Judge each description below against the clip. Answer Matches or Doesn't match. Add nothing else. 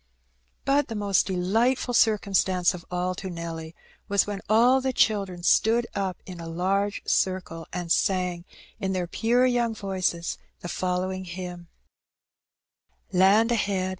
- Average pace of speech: Matches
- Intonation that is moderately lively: Matches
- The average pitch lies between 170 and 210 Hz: Matches